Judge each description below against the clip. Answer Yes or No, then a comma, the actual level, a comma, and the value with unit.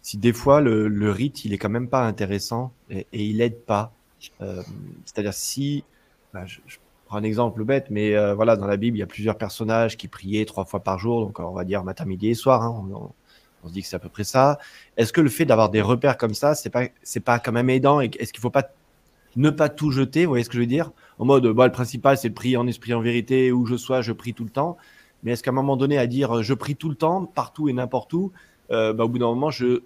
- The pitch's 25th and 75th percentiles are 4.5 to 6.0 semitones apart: No, average, 3.9 semitones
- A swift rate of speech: Yes, fast, 280 wpm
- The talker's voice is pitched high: No, low, 120 Hz